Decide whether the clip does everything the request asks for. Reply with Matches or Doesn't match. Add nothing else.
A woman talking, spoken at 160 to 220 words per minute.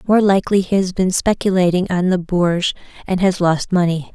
Matches